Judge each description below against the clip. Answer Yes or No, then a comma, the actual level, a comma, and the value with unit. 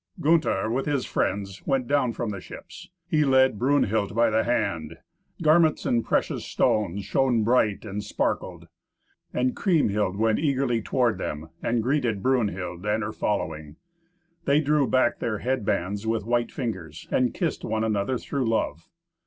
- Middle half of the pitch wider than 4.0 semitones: Yes, average, 4.5 semitones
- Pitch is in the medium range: No, low, 115 Hz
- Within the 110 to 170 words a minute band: Yes, average, 155 wpm